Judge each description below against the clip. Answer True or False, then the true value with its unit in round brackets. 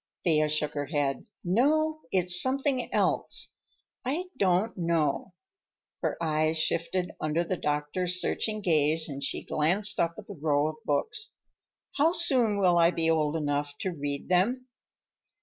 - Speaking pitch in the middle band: True (170 Hz)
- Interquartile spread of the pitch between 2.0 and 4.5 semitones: False (5.4 semitones)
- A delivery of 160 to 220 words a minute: False (150 wpm)